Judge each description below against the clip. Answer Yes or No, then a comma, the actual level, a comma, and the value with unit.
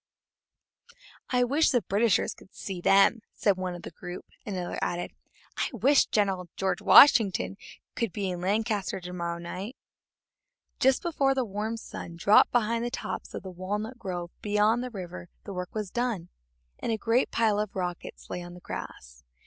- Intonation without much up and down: No, average, 4.4 semitones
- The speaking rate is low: No, average, 175 wpm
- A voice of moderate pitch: No, high, 200 Hz